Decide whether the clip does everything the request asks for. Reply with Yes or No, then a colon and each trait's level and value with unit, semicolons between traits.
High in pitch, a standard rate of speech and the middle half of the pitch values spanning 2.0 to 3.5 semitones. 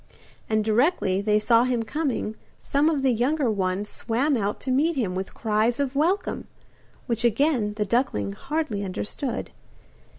No: high, 235 Hz; average, 155 wpm; average, 4.9 semitones